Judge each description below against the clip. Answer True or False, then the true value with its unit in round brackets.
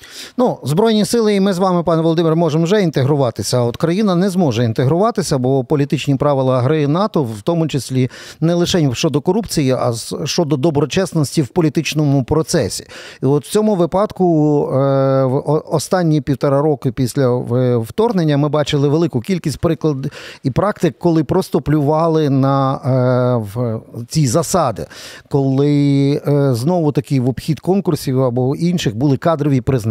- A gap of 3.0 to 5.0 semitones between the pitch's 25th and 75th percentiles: True (4.1 semitones)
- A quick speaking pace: False (140 wpm)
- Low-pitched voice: False (150 Hz)